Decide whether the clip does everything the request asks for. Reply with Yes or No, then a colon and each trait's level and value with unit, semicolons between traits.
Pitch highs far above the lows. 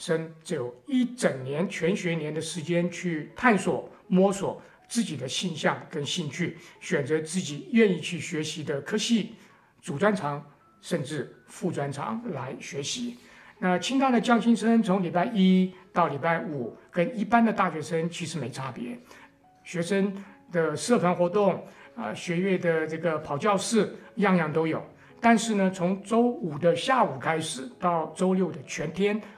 No: average, 4.2 semitones